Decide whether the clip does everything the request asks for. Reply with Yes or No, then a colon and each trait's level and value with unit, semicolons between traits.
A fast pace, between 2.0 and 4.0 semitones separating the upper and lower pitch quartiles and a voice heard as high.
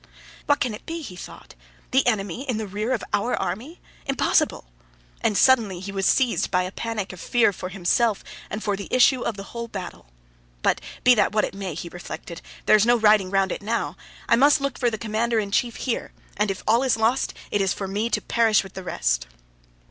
Yes: fast, 220 wpm; average, 3.6 semitones; high, 215 Hz